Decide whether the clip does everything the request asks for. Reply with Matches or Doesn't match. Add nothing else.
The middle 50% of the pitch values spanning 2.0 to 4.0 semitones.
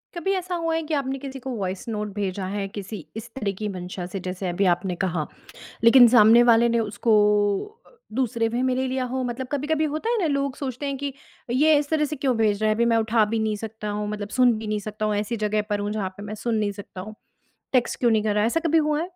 Doesn't match